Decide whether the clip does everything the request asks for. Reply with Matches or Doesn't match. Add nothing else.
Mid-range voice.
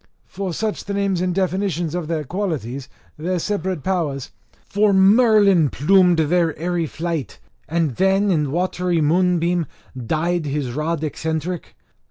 Matches